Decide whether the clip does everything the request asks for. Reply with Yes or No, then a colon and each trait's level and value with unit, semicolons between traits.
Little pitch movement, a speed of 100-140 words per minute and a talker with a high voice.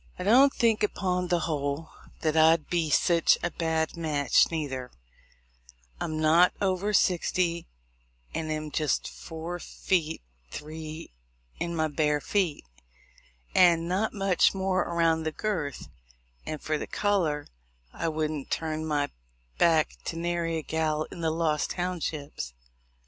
No: narrow, 2.3 semitones; slow, 135 wpm; medium, 160 Hz